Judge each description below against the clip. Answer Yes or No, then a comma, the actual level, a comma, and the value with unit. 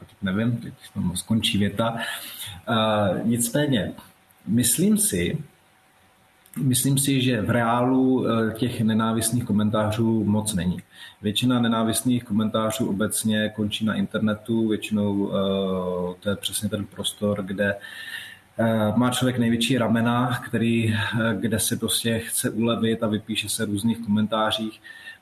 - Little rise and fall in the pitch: Yes, narrow, 2.1 semitones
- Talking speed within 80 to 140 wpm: Yes, average, 130 wpm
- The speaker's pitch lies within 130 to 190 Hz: No, low, 110 Hz